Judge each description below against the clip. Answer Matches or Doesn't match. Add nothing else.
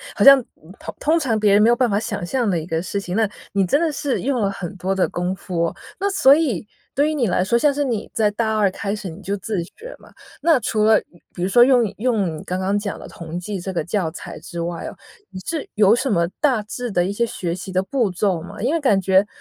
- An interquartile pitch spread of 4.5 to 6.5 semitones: Matches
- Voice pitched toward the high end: Matches